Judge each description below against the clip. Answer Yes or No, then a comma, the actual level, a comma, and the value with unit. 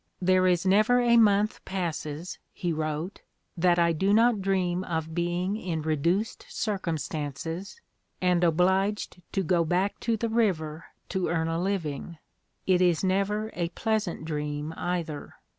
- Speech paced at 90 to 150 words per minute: Yes, average, 140 wpm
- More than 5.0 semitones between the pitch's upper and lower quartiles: No, average, 3.4 semitones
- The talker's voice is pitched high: No, medium, 180 Hz